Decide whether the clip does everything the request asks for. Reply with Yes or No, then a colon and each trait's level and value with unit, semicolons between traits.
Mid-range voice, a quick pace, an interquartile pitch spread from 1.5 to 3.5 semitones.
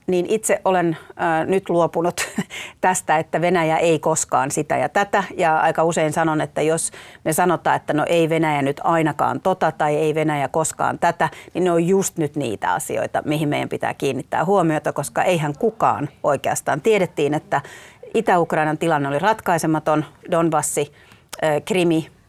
Yes: medium, 165 Hz; fast, 160 wpm; narrow, 2.6 semitones